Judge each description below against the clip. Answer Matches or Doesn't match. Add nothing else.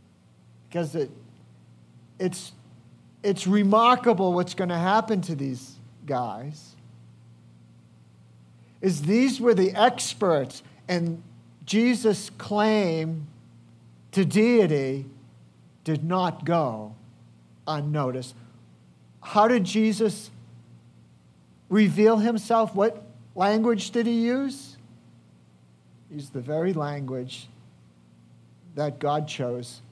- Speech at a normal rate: Doesn't match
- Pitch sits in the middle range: Matches